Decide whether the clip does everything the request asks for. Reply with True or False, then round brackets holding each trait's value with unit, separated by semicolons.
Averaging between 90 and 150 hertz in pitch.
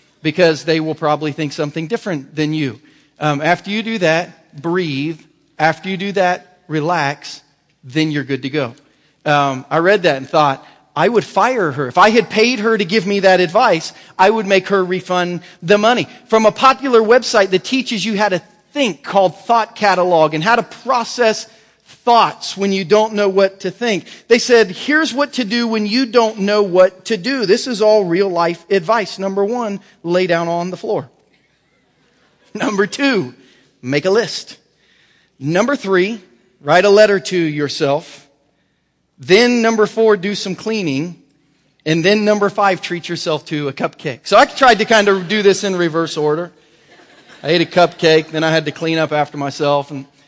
False (185 Hz)